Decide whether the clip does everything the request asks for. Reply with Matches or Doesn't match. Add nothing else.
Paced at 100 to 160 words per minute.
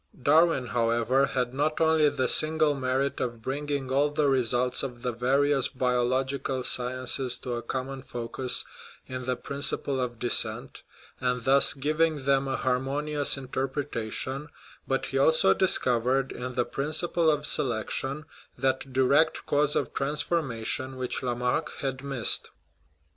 Matches